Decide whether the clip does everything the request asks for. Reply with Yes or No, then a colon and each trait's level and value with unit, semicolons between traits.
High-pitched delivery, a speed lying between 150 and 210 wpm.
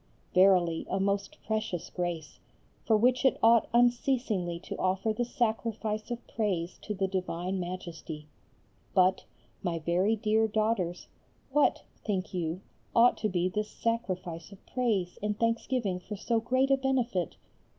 No: high, 205 Hz; average, 140 wpm